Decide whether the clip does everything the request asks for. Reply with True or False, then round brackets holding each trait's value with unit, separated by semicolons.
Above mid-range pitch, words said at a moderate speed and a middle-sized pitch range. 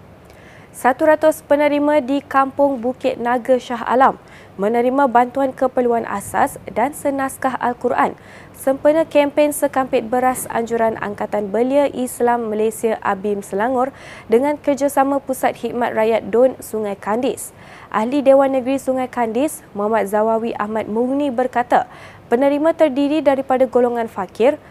True (255 Hz; 120 wpm; 3.3 semitones)